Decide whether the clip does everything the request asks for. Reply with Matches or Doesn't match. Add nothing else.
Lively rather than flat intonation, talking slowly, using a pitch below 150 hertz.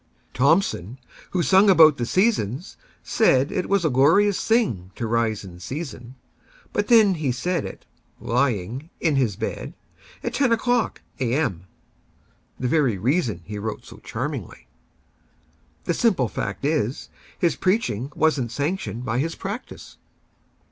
Matches